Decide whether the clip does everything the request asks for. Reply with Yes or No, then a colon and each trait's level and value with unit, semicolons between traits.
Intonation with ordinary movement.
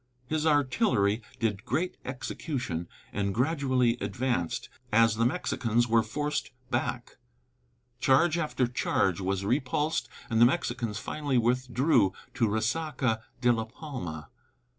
Yes: average, 4.5 semitones